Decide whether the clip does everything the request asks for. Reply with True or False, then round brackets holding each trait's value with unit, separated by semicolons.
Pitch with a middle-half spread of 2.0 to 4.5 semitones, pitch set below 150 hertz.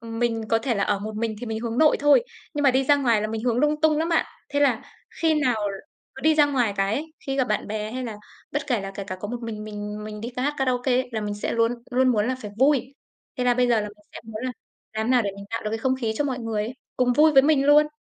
False (4.0 semitones; 245 Hz)